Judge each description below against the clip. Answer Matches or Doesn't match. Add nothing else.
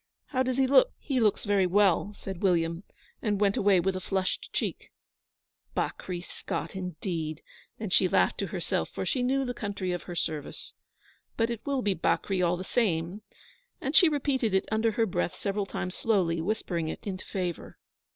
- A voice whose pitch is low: Doesn't match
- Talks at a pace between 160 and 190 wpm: Matches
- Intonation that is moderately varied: Matches